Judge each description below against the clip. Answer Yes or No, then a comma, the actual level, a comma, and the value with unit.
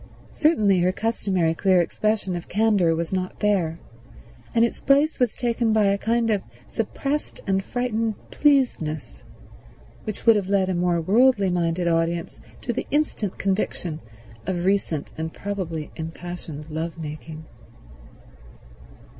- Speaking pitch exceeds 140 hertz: Yes, high, 190 Hz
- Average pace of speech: No, slow, 130 wpm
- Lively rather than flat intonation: No, average, 4.9 semitones